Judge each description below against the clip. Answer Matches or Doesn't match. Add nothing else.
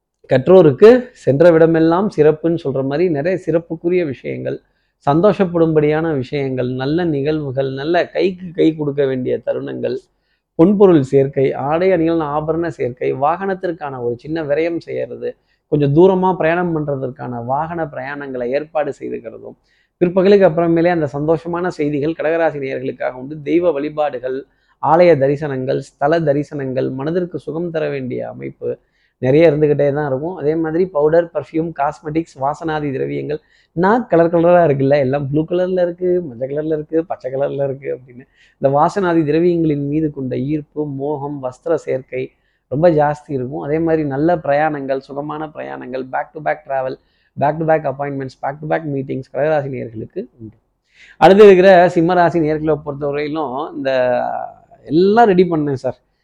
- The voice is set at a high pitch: Doesn't match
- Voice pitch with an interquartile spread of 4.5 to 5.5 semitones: Doesn't match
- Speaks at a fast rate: Matches